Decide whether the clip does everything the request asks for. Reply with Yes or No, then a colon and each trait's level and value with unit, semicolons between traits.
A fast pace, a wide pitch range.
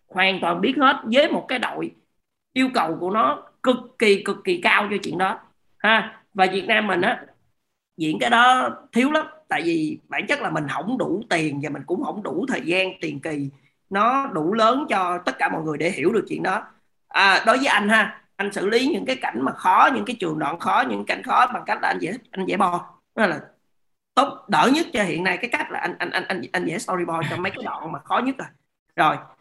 No: average, 240 wpm; wide, 6.5 semitones